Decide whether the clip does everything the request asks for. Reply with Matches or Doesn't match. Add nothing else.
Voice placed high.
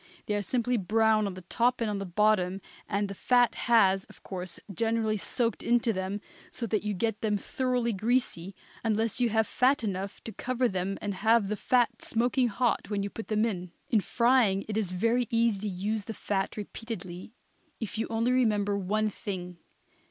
Matches